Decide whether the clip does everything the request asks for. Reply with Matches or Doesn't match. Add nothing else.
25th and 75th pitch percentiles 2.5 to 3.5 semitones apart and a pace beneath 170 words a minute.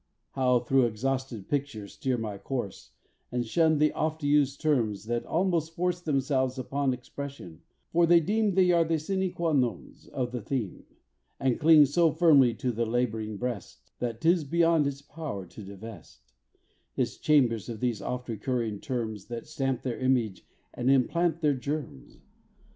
Doesn't match